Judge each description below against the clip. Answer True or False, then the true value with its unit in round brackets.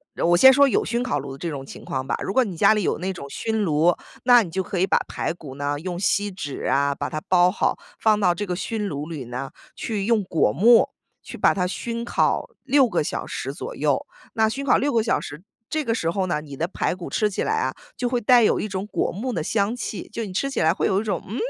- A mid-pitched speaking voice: False (195 Hz)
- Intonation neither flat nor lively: False (5.9 semitones)